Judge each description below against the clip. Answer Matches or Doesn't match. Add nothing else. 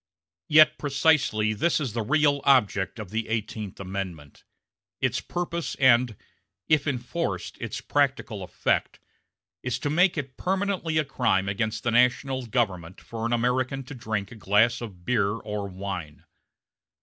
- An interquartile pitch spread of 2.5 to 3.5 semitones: Doesn't match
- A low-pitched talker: Matches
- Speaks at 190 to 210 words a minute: Doesn't match